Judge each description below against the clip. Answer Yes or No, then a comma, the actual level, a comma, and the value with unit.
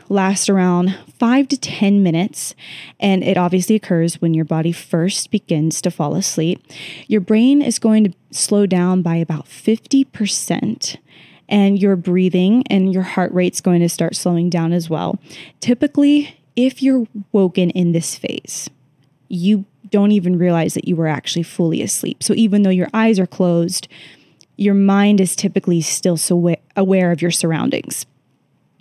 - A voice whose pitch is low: No, medium, 185 Hz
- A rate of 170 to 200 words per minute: No, average, 155 wpm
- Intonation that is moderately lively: Yes, average, 3.2 semitones